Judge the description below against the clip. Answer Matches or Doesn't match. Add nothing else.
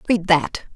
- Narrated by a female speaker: Matches